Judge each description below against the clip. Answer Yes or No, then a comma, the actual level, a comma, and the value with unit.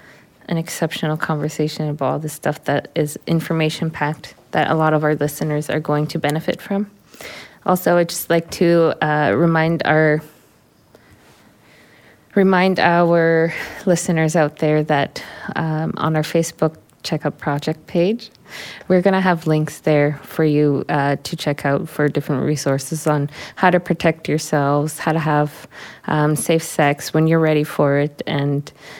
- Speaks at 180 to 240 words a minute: No, average, 155 wpm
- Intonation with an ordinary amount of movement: No, narrow, 2.1 semitones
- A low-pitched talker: No, medium, 155 Hz